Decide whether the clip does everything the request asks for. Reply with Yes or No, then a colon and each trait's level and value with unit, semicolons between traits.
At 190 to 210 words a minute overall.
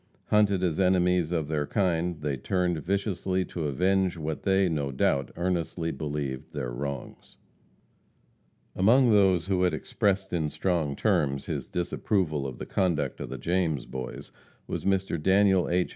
No: average, 150 wpm